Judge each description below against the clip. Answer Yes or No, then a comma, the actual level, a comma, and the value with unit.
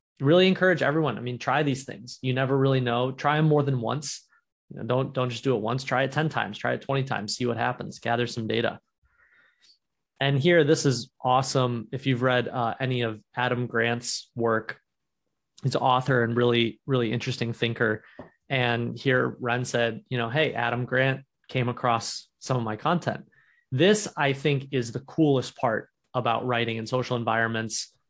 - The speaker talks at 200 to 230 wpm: No, average, 185 wpm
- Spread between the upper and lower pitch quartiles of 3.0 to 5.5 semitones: No, narrow, 2.4 semitones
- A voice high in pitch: No, low, 125 Hz